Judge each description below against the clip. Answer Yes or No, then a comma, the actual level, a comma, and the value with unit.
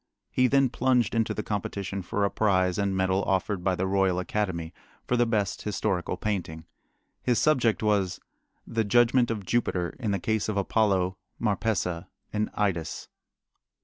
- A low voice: Yes, low, 100 Hz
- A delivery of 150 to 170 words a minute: Yes, average, 155 wpm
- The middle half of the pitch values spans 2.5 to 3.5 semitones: Yes, average, 3.1 semitones